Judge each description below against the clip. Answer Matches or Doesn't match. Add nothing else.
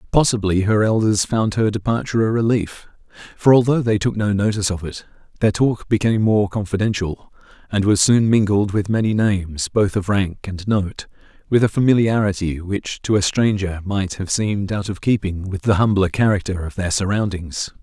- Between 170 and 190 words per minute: Matches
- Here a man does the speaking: Matches